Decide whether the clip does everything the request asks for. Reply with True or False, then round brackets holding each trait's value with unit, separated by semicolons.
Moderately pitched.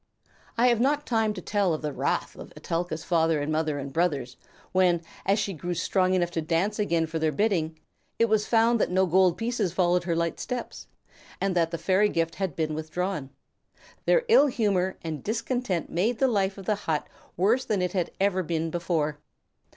True (180 Hz)